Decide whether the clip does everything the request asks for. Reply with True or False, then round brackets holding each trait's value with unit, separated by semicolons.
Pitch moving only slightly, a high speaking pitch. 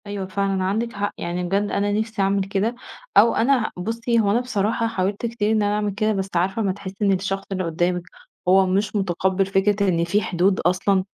True (2.0 semitones; 200 Hz)